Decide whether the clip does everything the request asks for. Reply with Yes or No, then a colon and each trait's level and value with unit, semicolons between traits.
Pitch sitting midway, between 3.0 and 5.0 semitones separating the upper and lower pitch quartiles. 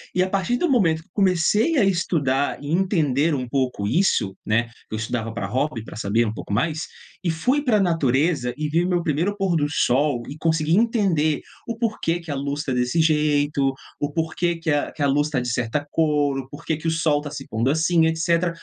Yes: medium, 155 Hz; average, 4.1 semitones